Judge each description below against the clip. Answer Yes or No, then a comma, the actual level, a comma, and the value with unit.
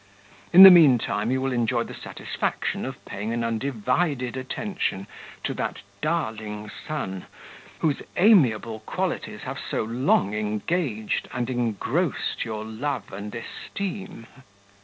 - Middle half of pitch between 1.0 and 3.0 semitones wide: No, wide, 5.4 semitones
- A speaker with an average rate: No, slow, 125 wpm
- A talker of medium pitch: No, low, 120 Hz